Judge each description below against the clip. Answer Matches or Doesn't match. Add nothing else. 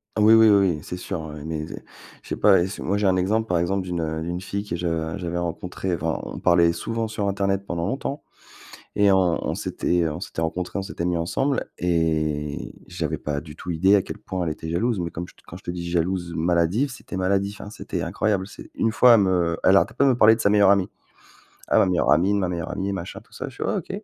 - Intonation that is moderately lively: Matches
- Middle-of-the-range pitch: Doesn't match